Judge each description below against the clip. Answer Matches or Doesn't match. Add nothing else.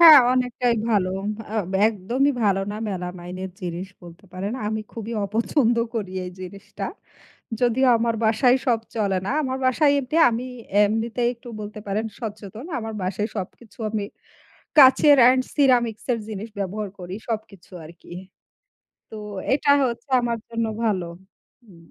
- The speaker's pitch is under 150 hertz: Doesn't match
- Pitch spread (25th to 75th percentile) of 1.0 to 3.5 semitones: Doesn't match